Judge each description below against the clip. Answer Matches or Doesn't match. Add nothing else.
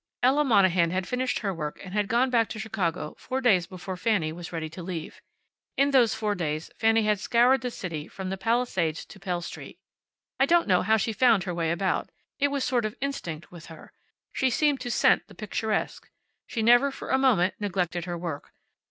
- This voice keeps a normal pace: Doesn't match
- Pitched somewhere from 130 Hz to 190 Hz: Doesn't match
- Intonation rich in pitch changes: Matches